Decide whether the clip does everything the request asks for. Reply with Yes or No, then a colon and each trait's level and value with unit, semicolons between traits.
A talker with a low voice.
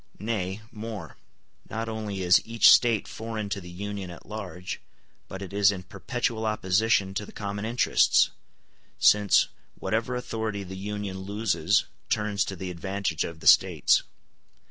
Yes: low, 100 Hz